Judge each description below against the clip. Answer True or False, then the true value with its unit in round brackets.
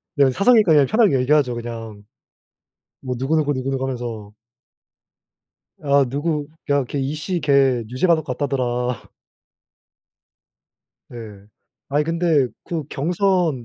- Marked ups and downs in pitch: False (3.9 semitones)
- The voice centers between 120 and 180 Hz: True (140 Hz)